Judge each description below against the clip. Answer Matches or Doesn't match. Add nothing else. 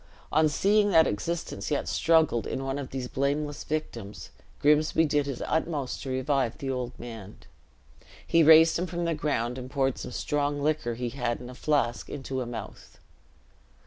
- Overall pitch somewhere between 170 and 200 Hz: Doesn't match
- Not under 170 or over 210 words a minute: Matches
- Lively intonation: Doesn't match